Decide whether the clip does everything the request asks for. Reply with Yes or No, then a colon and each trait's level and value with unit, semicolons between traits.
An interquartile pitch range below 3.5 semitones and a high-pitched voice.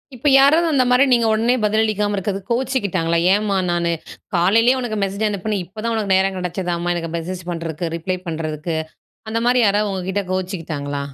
No: average, 4.1 semitones; high, 195 Hz